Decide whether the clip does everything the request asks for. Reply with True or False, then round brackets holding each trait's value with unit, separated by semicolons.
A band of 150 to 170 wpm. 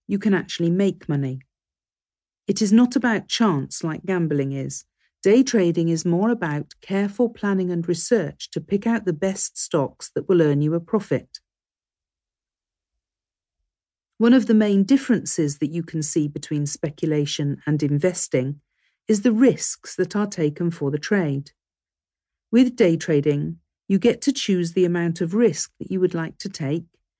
True (160 wpm)